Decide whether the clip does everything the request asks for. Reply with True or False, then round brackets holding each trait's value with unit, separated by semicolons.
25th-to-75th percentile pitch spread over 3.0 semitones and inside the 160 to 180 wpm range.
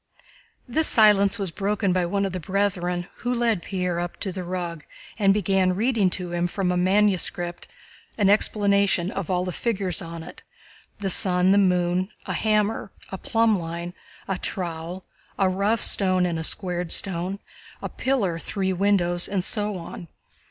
False (2.4 semitones; 170 wpm)